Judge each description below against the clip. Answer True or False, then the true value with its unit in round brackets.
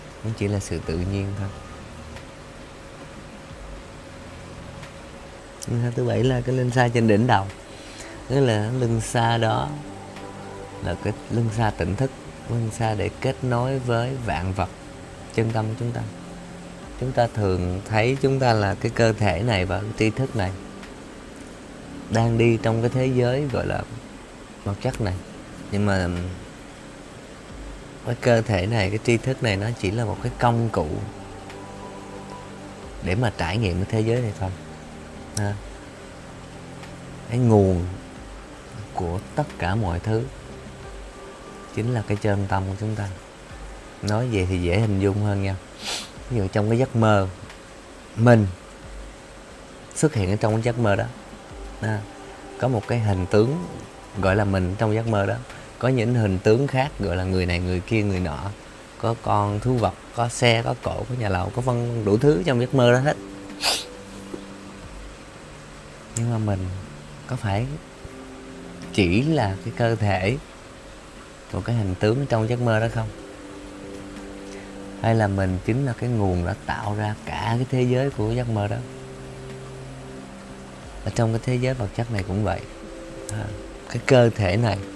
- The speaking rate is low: True (160 wpm)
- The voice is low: True (105 Hz)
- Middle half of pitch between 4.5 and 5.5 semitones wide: False (3.3 semitones)